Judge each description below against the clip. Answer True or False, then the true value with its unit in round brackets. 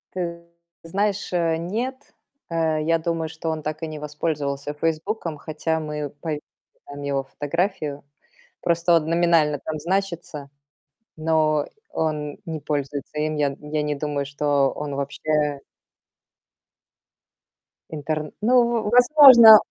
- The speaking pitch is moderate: True (155 Hz)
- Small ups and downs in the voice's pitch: True (2.3 semitones)